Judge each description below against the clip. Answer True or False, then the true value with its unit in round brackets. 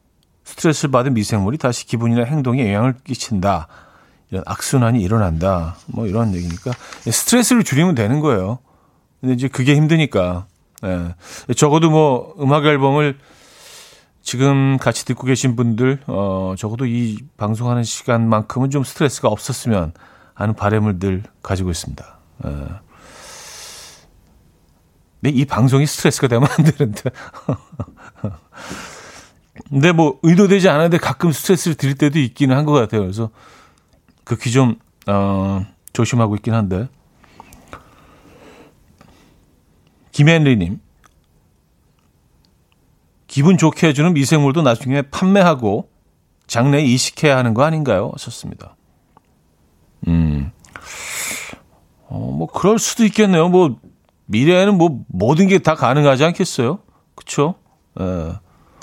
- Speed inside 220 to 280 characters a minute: True (260 characters per minute)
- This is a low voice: True (125 Hz)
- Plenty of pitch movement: True (7.1 semitones)